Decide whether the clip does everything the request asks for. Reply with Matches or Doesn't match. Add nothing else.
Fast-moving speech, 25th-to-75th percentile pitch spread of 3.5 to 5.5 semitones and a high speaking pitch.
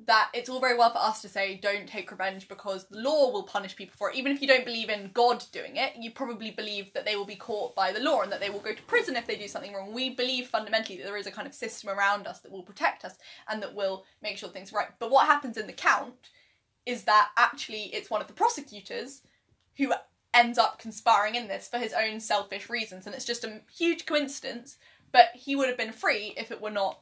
Matches